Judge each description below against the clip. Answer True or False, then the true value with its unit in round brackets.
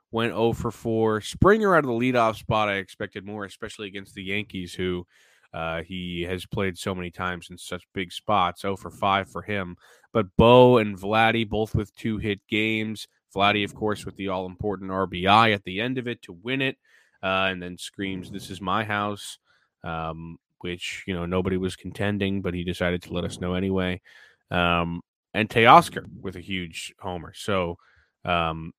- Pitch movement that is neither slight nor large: True (3.1 semitones)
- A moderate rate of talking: True (190 wpm)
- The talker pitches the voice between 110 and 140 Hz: False (95 Hz)